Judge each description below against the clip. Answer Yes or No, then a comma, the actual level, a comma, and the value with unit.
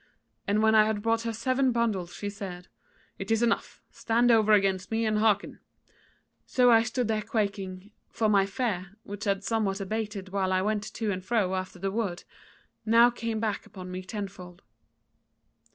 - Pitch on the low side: No, high, 210 Hz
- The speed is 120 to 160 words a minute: No, average, 175 wpm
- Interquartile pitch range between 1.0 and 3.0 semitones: Yes, average, 2.7 semitones